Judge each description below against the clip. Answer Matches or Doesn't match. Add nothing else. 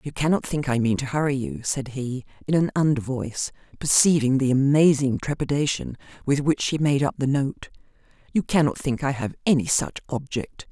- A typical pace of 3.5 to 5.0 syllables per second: Doesn't match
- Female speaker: Matches